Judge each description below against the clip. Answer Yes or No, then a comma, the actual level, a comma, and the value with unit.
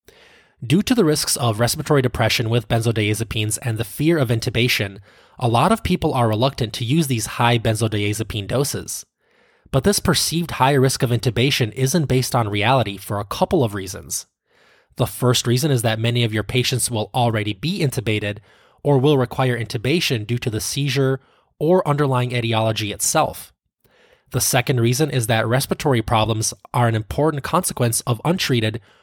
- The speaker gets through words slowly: No, average, 165 wpm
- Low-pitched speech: Yes, low, 125 Hz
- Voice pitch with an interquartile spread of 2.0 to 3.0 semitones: No, average, 4.0 semitones